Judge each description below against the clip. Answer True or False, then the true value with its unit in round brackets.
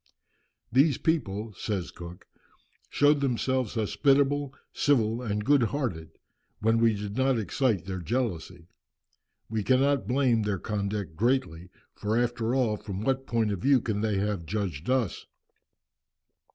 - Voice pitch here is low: True (110 Hz)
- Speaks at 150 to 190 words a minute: False (135 wpm)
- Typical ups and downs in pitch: True (4.5 semitones)